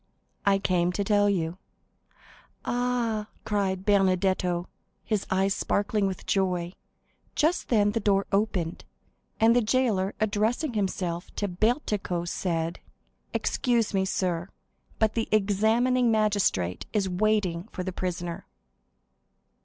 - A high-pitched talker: Yes, high, 200 Hz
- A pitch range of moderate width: Yes, average, 3.0 semitones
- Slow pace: Yes, slow, 115 wpm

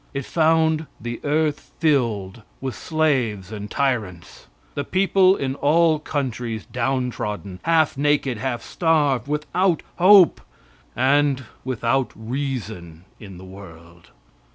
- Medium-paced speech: No, slow, 110 wpm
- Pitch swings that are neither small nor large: No, wide, 5.8 semitones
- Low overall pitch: Yes, low, 130 Hz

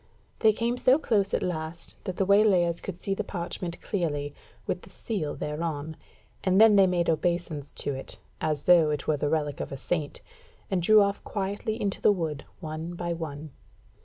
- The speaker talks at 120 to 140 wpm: No, average, 190 wpm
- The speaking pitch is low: No, medium, 175 Hz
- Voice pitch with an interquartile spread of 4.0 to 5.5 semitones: Yes, average, 4.3 semitones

